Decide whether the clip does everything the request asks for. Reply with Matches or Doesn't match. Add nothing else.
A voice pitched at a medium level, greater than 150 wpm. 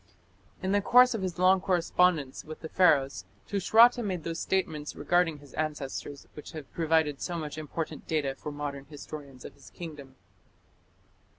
Matches